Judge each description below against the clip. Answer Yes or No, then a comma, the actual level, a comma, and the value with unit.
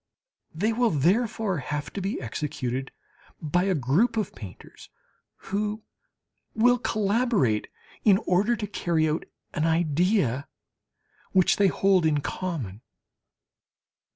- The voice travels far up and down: Yes, wide, 6.1 semitones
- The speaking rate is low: Yes, slow, 115 wpm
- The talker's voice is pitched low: No, medium, 180 Hz